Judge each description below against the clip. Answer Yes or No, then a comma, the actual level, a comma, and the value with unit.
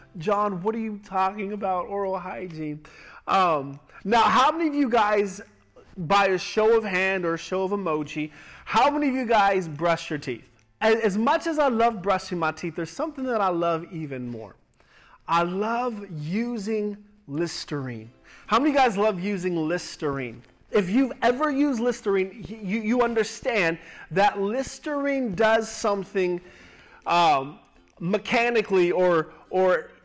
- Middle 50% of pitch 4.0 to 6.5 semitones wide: Yes, average, 4.8 semitones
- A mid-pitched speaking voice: No, high, 195 Hz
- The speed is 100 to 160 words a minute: Yes, average, 150 wpm